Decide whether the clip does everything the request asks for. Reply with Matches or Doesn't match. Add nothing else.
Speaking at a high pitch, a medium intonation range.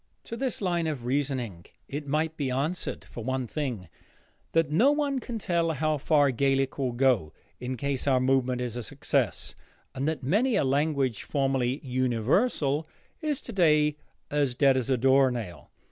Doesn't match